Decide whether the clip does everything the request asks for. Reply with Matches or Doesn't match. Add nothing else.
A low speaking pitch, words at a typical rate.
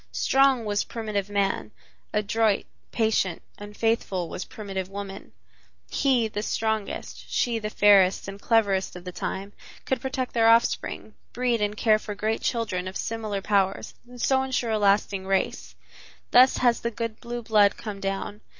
Doesn't match